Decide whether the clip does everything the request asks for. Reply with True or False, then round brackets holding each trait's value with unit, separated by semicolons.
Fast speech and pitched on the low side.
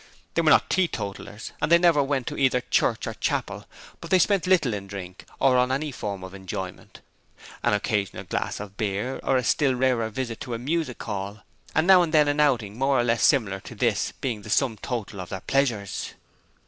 True (210 wpm; 120 Hz)